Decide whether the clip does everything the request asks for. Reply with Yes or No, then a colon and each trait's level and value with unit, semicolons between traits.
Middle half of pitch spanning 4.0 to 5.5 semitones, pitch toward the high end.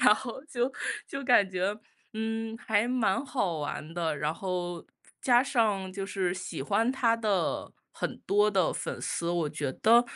Yes: average, 4.5 semitones; high, 205 Hz